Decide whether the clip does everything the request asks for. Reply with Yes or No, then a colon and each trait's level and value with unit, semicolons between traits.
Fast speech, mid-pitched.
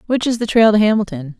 No: fast, 260 wpm; high, 210 Hz